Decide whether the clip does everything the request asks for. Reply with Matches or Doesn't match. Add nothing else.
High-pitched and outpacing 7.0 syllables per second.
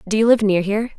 Matches